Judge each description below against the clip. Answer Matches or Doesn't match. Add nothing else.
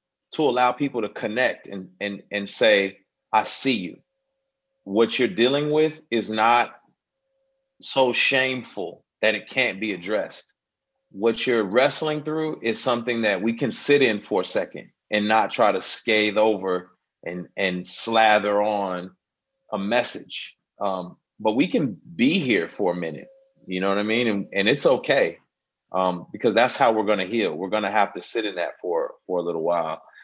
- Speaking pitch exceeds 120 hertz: Doesn't match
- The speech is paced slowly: Doesn't match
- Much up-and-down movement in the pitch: Matches